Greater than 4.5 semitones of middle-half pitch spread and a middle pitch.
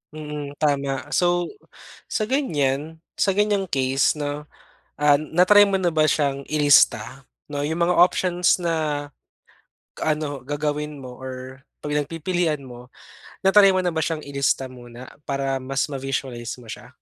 No: average, 3.9 semitones; medium, 150 Hz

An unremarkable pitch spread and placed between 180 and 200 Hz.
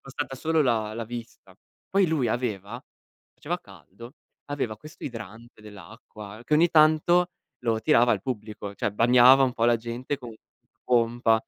No: average, 3.4 semitones; low, 120 Hz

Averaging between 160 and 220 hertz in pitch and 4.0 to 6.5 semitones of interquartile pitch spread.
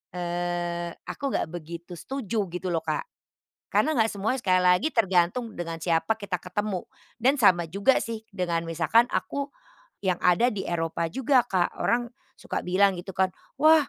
Yes: medium, 185 Hz; average, 4.6 semitones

